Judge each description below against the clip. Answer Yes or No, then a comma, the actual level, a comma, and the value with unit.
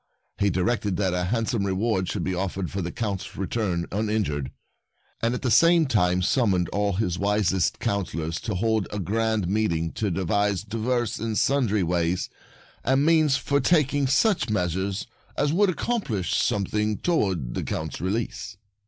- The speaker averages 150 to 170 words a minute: Yes, average, 160 wpm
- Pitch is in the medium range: No, low, 105 Hz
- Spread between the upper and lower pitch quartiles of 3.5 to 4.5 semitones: Yes, average, 4.2 semitones